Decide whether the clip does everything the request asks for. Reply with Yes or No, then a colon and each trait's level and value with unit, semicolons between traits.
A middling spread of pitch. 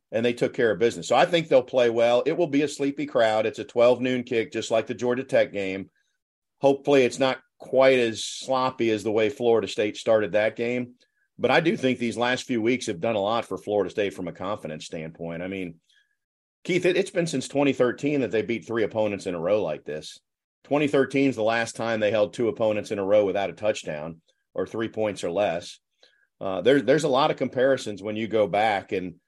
Yes: average, 3.7 semitones